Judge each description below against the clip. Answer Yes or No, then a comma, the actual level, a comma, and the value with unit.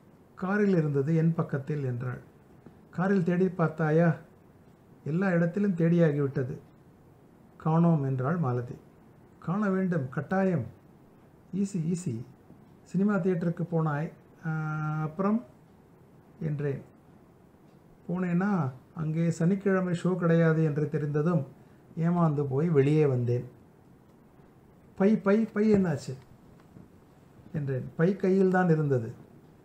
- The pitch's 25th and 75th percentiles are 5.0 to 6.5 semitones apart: No, average, 3.7 semitones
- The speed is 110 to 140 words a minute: No, average, 90 wpm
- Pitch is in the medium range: Yes, medium, 165 Hz